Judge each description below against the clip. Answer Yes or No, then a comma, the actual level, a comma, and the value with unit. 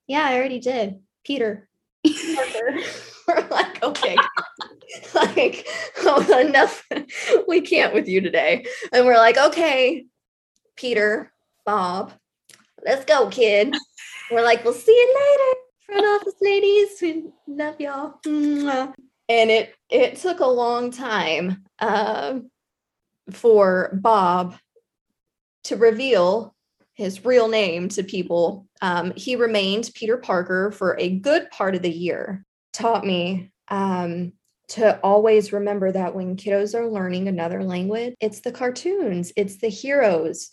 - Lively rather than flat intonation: Yes, wide, 6.8 semitones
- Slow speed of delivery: Yes, slow, 125 wpm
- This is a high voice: Yes, high, 230 Hz